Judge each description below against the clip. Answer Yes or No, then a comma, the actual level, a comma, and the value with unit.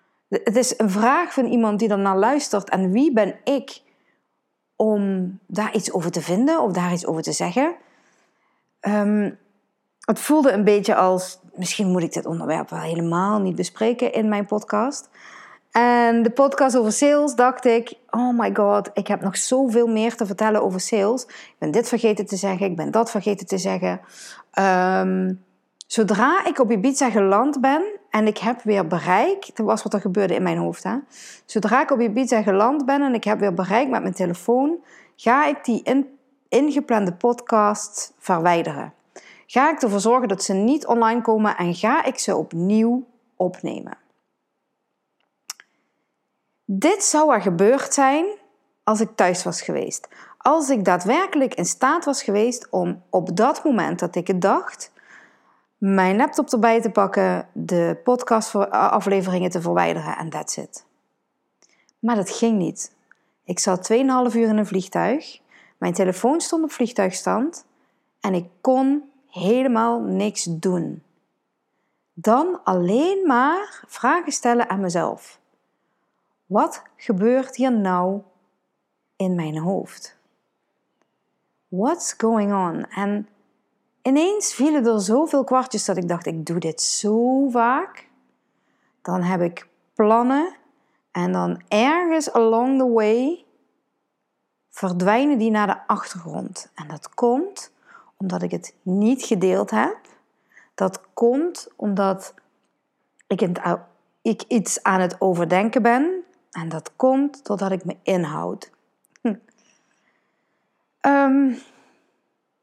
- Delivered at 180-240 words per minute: No, average, 140 wpm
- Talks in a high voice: Yes, high, 220 Hz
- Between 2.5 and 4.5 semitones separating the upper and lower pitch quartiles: No, average, 5.2 semitones